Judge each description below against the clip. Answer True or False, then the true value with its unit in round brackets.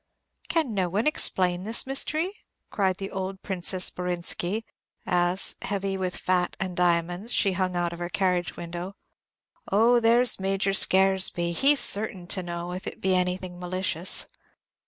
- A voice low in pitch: False (185 Hz)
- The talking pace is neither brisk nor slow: True (155 wpm)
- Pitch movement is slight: True (2.0 semitones)